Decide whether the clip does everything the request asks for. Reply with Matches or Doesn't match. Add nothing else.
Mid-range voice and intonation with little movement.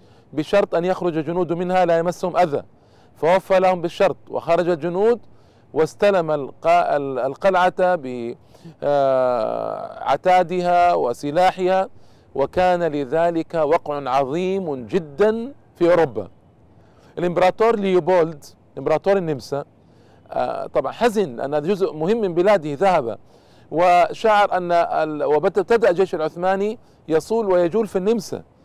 Doesn't match